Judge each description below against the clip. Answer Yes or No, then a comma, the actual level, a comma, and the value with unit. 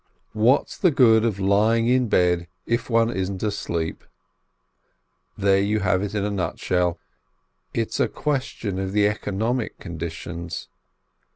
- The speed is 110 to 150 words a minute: Yes, slow, 135 wpm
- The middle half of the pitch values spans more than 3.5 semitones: Yes, average, 3.9 semitones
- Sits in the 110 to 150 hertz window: No, low, 100 Hz